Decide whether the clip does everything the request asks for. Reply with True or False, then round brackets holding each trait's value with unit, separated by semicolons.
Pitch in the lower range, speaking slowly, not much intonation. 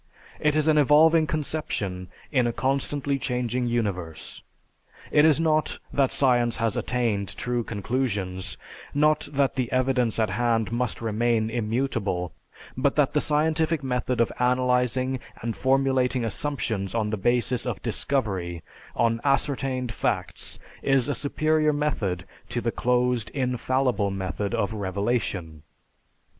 False (125 Hz; 130 wpm; 3.9 semitones)